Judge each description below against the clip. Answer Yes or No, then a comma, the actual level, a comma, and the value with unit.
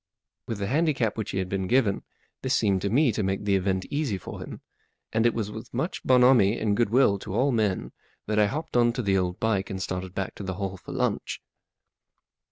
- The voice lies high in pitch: No, low, 105 Hz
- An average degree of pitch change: Yes, average, 3.8 semitones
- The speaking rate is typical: No, fast, 220 wpm